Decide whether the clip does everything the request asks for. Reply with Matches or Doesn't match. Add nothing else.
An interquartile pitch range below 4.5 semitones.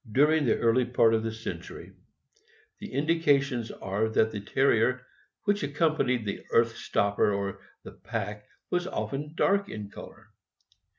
Doesn't match